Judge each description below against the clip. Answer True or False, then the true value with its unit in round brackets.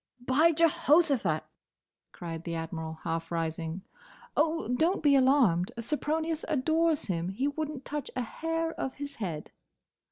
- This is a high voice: True (265 Hz)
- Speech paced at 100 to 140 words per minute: True (135 wpm)